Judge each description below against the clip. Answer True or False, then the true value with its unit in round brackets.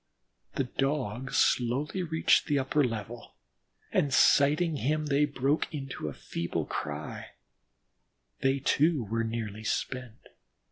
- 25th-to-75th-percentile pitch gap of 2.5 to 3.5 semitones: False (4.4 semitones)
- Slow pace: True (120 wpm)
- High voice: False (135 Hz)